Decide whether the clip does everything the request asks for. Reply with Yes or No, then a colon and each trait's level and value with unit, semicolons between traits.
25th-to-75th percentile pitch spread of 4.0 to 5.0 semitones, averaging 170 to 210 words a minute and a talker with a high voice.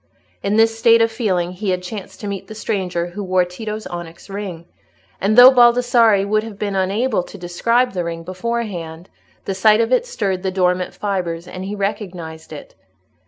No: average, 3.6 semitones; average, 185 wpm; high, 195 Hz